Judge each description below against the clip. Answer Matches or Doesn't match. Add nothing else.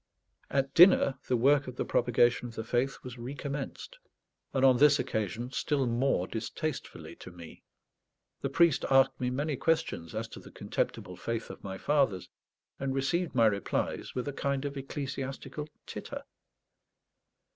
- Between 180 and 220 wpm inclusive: Doesn't match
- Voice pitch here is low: Matches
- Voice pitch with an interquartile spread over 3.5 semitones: Doesn't match